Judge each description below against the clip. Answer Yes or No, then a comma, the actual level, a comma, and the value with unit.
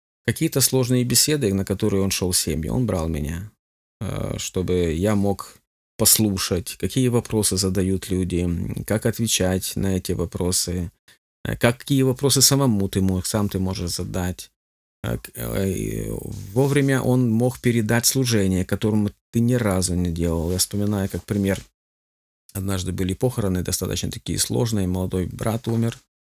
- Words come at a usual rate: Yes, average, 130 wpm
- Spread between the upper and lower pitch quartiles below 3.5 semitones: No, average, 4.3 semitones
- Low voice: Yes, low, 100 Hz